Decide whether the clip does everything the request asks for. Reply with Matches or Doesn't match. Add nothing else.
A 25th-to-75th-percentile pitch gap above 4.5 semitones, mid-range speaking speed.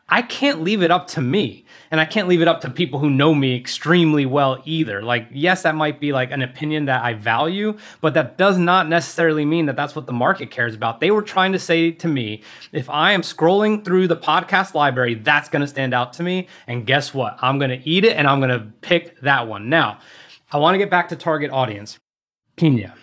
Doesn't match